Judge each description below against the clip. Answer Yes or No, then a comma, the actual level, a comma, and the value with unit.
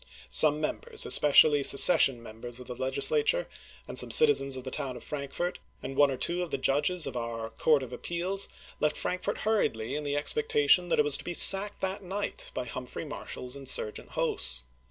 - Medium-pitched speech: Yes, medium, 145 Hz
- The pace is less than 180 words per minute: No, average, 185 wpm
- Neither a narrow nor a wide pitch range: No, wide, 6.0 semitones